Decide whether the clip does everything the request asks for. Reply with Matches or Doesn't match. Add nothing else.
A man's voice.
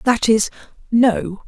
Doesn't match